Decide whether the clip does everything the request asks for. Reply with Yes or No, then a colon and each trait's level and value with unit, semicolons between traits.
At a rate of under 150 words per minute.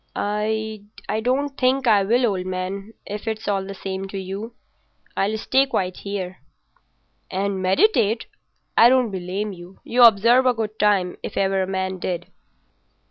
No: average, 155 wpm